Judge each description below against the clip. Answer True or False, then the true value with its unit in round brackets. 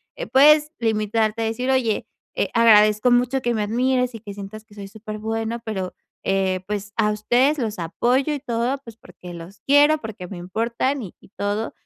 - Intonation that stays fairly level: False (3.3 semitones)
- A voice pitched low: False (225 Hz)